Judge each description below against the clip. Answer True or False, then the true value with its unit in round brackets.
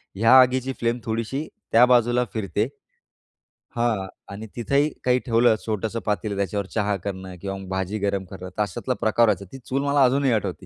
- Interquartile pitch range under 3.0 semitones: False (3.7 semitones)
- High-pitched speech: False (110 Hz)